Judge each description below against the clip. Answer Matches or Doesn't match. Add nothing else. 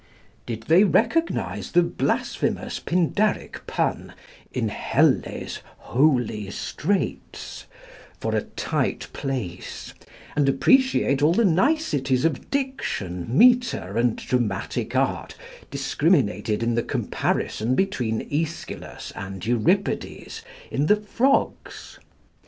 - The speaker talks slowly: Matches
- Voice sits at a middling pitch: Matches